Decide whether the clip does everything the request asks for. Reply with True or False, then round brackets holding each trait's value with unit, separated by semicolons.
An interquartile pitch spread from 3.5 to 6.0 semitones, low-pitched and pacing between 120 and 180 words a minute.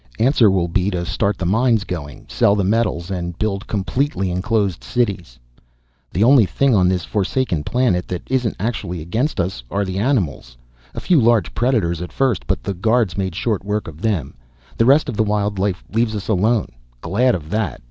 False (4.4 semitones; 100 Hz; 190 wpm)